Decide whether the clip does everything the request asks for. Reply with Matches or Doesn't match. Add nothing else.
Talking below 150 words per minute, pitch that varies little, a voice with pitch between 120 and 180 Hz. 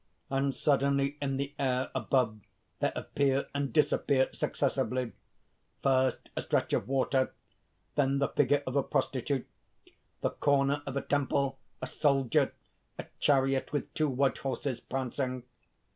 Matches